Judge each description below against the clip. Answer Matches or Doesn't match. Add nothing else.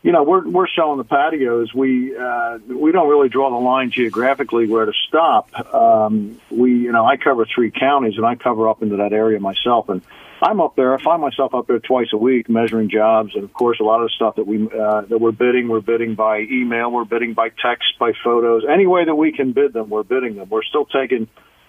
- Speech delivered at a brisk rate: Matches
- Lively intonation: Doesn't match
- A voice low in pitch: Matches